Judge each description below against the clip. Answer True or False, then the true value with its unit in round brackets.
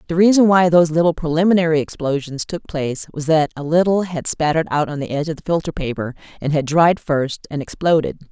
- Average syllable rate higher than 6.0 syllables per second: True (6.2 syllables/s)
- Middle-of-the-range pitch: True (160 Hz)